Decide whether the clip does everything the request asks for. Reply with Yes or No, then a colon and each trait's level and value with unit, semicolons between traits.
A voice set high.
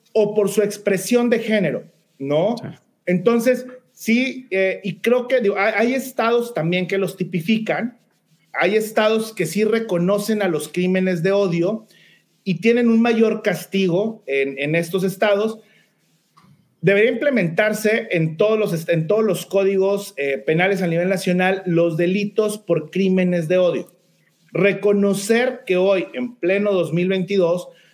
Yes: high, 195 Hz